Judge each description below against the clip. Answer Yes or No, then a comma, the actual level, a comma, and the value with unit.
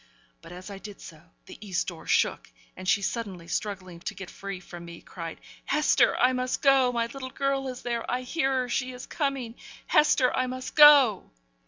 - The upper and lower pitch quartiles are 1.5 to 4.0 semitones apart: No, wide, 5.4 semitones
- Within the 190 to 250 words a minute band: Yes, average, 195 wpm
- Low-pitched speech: No, high, 240 Hz